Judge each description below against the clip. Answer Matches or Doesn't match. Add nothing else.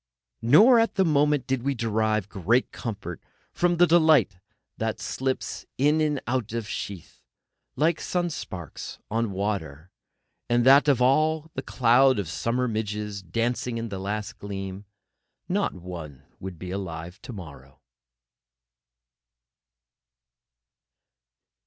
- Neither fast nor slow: Doesn't match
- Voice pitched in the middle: Doesn't match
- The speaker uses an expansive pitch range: Matches